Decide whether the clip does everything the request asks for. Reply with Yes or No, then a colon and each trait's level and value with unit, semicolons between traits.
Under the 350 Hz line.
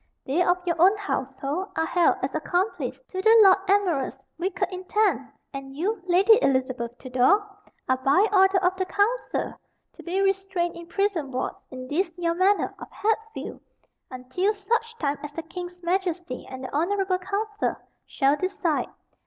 No: very high, 360 Hz